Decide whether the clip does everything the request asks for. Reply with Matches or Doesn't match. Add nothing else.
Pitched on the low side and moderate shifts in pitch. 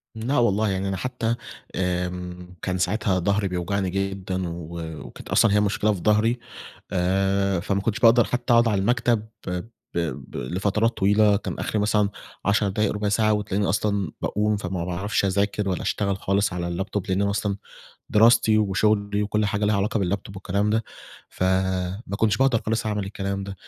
Doesn't match